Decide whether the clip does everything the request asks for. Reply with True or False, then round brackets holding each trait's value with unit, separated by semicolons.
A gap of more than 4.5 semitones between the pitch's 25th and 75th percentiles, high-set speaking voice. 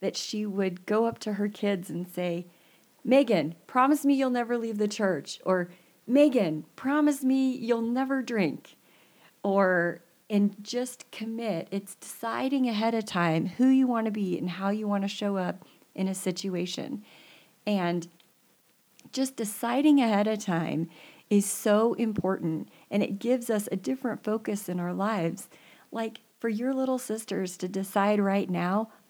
False (4.0 semitones; 205 Hz)